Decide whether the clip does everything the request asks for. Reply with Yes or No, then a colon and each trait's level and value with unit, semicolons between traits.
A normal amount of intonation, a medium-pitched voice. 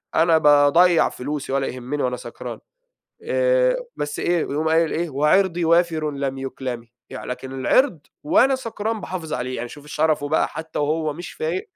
Yes: average, 4.0 semitones; medium, 155 Hz